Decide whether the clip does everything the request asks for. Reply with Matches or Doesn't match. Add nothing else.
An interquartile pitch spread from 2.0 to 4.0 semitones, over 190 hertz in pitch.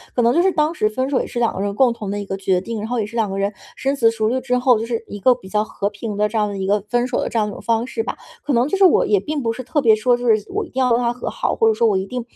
Matches